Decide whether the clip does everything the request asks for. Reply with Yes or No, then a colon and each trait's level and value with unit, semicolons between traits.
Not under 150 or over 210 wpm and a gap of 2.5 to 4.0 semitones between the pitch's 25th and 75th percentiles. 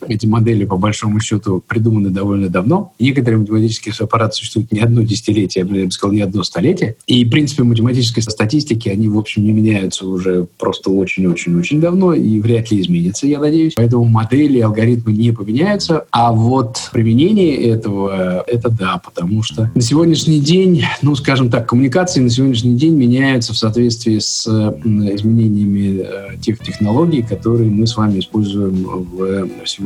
Yes: fast, 160 wpm; average, 3.5 semitones